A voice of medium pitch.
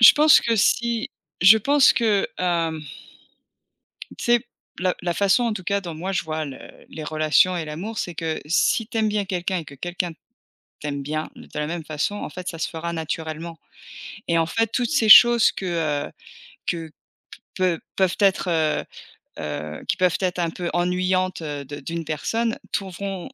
Yes: medium, 175 Hz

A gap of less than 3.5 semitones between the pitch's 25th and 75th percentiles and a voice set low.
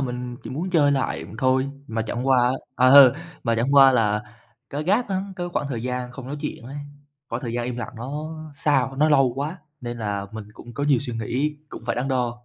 Yes: average, 3.0 semitones; low, 130 Hz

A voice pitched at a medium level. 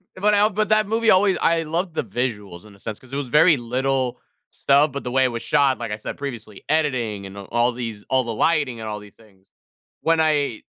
No: low, 130 Hz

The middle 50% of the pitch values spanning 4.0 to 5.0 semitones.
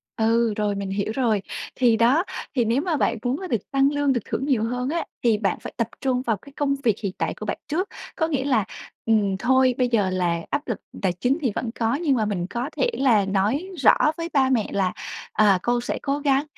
Yes: average, 4.5 semitones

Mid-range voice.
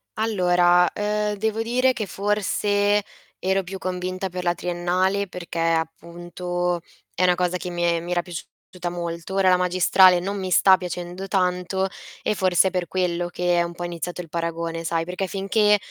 Yes: medium, 180 Hz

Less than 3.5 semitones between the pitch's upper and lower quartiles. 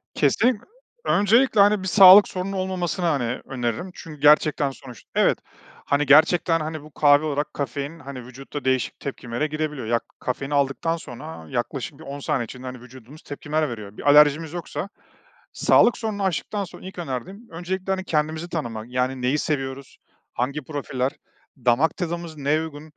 No: average, 4.4 semitones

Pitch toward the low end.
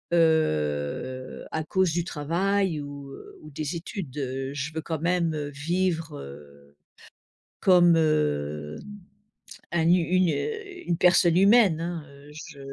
No: medium, 160 Hz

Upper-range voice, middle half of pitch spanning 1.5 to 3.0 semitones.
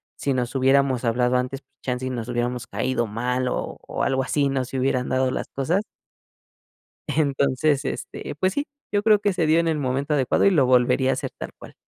No: low, 130 Hz; average, 2.7 semitones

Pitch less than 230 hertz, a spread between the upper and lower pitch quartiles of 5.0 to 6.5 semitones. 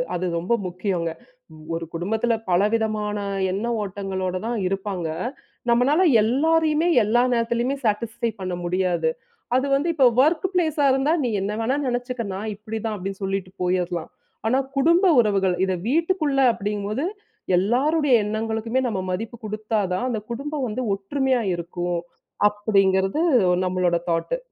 Yes: high, 215 Hz; wide, 5.5 semitones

